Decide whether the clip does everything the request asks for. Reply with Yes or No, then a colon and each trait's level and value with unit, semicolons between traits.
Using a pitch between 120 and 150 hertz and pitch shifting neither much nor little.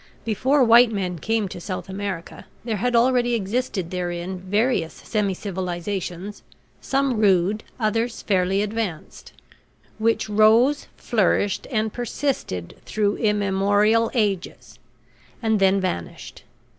No: high, 205 Hz; average, 3.3 semitones